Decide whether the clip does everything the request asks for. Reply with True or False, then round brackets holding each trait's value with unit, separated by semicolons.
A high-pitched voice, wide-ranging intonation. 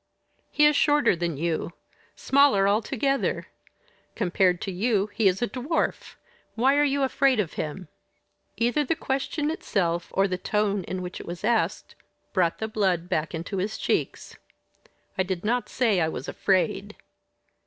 True (205 Hz; 6.1 semitones)